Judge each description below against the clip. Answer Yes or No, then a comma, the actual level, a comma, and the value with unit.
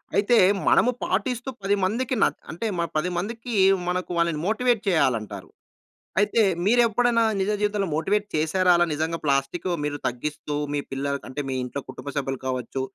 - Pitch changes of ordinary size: No, wide, 7.3 semitones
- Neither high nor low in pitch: Yes, medium, 180 Hz